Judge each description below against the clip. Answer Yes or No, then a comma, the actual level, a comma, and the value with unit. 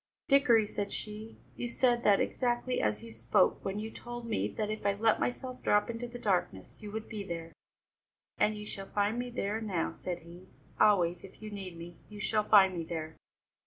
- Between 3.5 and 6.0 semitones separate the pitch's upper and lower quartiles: Yes, average, 3.9 semitones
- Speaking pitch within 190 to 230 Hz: Yes, high, 210 Hz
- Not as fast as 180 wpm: No, average, 200 wpm